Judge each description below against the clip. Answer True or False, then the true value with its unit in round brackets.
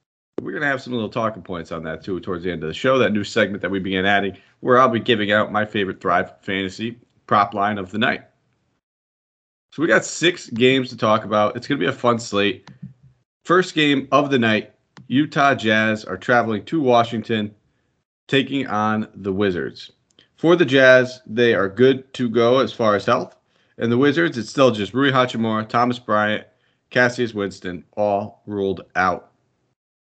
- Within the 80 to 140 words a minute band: False (190 wpm)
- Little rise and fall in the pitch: False (3.9 semitones)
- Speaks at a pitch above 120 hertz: False (115 Hz)